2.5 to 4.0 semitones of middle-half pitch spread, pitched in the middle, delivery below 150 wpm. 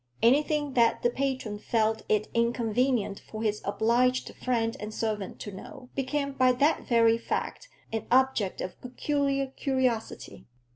No: average, 3.3 semitones; high, 240 Hz; average, 140 wpm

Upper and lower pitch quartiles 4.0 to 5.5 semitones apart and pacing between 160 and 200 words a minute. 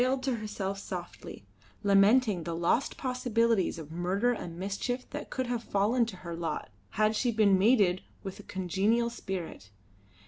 Yes: average, 4.4 semitones; average, 165 wpm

